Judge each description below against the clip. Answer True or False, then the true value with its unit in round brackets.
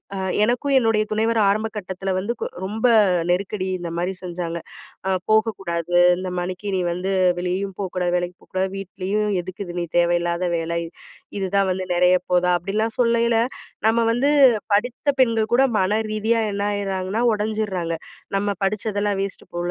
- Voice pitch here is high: True (195 Hz)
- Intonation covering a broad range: False (3.2 semitones)